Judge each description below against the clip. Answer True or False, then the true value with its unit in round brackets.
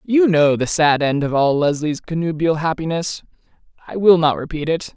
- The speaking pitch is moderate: True (160 Hz)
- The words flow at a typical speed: True (180 wpm)